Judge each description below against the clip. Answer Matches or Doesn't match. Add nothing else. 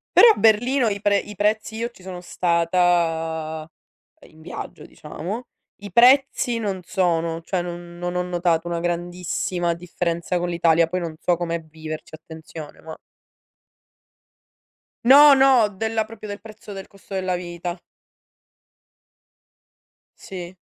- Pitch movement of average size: Matches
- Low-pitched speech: Doesn't match